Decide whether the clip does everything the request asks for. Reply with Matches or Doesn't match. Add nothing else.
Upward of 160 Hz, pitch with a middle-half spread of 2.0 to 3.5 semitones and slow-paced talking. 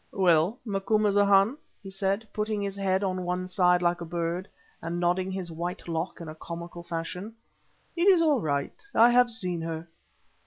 Doesn't match